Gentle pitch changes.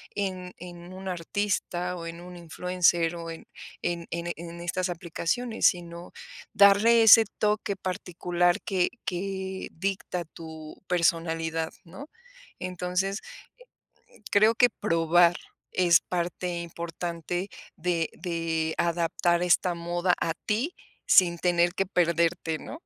Yes: narrow, 1.8 semitones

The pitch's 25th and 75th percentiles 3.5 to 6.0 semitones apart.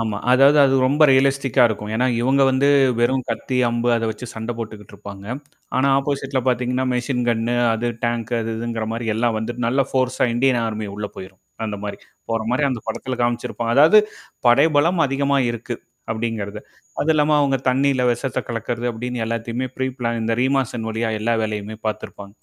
No: average, 2.9 semitones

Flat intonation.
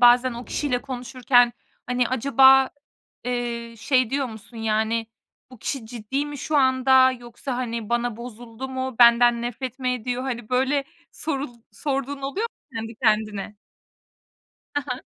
Yes: narrow, 2.1 semitones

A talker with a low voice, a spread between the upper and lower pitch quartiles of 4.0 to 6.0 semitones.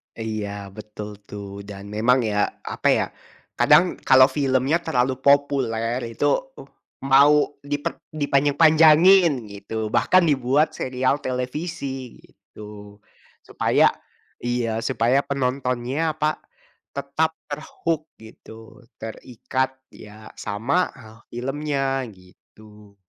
Yes: low, 130 Hz; average, 4.4 semitones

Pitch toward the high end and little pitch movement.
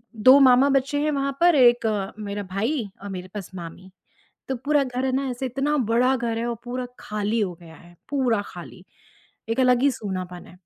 No: high, 240 Hz; average, 4.7 semitones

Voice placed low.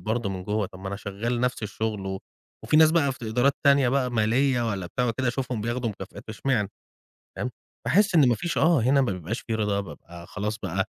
Yes: low, 115 Hz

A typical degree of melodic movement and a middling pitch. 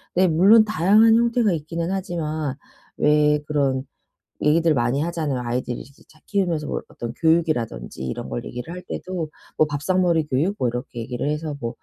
Yes: average, 5.0 semitones; medium, 155 Hz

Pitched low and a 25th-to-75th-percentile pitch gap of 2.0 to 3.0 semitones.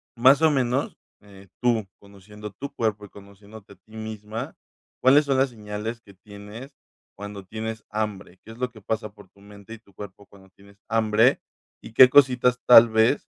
Yes: low, 110 Hz; average, 2.7 semitones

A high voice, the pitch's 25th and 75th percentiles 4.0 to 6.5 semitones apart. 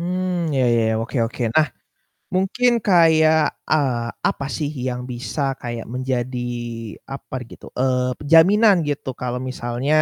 No: medium, 140 Hz; average, 4.7 semitones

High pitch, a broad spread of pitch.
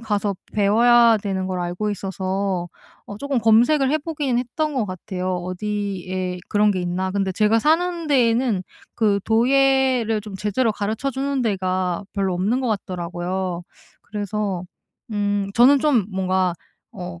No: high, 205 Hz; average, 4.4 semitones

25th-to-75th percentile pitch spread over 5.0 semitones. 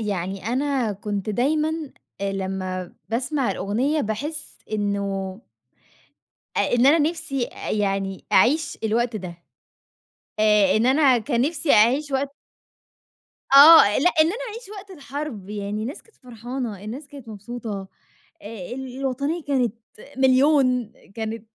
Yes: wide, 5.5 semitones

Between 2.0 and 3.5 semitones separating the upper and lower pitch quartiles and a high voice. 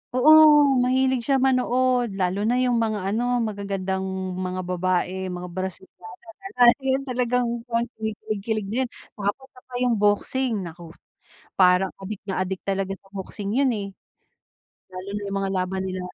No: average, 4.7 semitones; high, 205 Hz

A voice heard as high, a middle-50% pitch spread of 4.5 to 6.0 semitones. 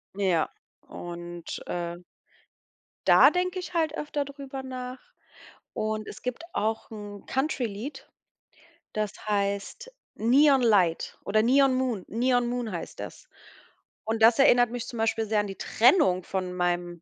Yes: high, 225 Hz; average, 4.8 semitones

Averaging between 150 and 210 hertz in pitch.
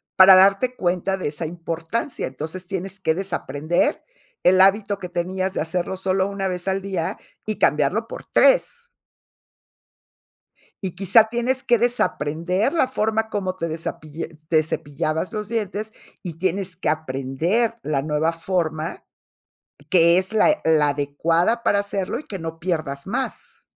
Yes: medium, 185 Hz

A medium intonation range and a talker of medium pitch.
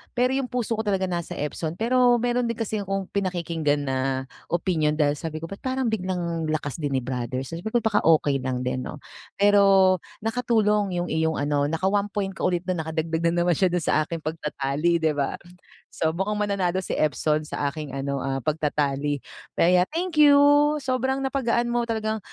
No: wide, 6.0 semitones; medium, 175 Hz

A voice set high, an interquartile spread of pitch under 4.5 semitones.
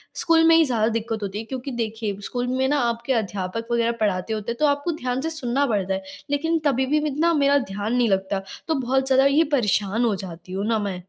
No: high, 235 Hz; average, 5.0 semitones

